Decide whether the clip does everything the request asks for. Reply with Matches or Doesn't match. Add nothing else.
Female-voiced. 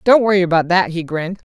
Matches